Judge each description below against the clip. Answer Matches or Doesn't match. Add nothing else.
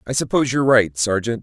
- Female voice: Doesn't match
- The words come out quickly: Matches